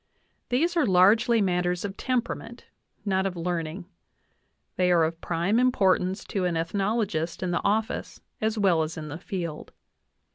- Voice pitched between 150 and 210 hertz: Yes, medium, 185 Hz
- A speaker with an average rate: Yes, average, 155 wpm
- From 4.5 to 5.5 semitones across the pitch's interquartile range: No, average, 3.8 semitones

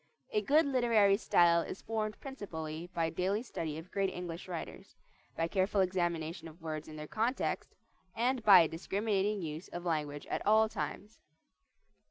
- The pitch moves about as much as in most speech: Yes, average, 4.7 semitones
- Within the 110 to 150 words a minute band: No, average, 160 wpm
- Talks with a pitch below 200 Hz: Yes, medium, 185 Hz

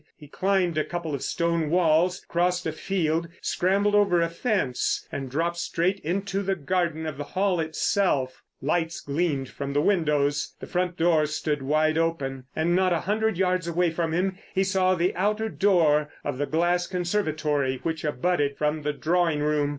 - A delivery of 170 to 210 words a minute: Yes, average, 175 wpm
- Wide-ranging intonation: No, average, 3.4 semitones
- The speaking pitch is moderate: Yes, medium, 170 Hz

